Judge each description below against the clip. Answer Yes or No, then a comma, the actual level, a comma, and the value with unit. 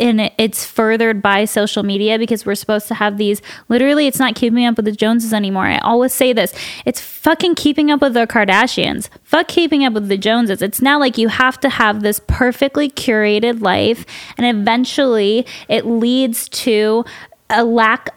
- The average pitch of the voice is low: No, high, 230 Hz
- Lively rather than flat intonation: No, average, 3.2 semitones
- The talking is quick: No, average, 190 wpm